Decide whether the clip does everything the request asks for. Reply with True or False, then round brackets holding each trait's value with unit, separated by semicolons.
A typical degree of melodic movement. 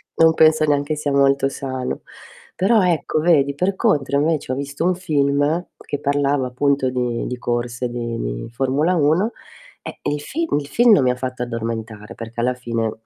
True (3.9 semitones)